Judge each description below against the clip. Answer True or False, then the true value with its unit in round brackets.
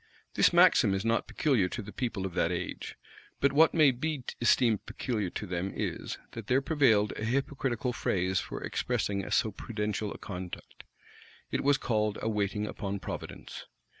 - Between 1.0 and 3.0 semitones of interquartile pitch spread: False (4.3 semitones)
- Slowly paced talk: False (165 wpm)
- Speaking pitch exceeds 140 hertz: False (110 Hz)